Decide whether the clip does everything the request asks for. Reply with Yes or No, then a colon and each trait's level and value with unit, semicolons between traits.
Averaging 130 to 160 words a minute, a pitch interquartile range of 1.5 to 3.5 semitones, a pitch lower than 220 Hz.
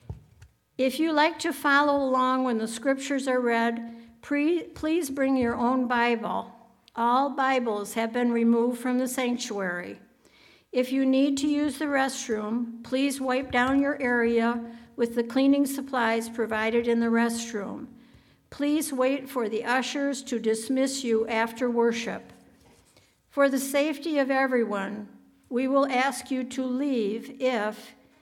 No: average, 140 wpm; average, 2.7 semitones; very high, 250 Hz